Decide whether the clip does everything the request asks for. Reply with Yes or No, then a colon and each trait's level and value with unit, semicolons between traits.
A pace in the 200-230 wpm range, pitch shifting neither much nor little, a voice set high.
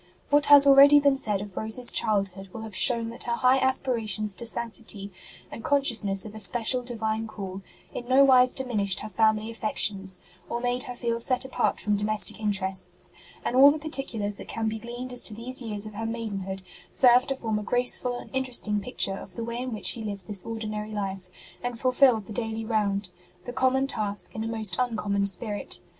Yes: fast, 205 wpm; average, 3.2 semitones; high, 225 Hz